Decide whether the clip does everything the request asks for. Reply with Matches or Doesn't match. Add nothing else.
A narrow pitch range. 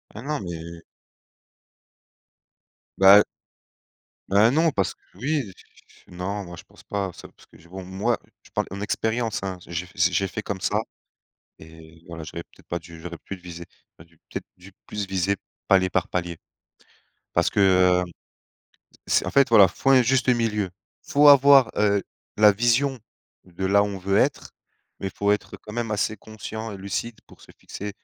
Doesn't match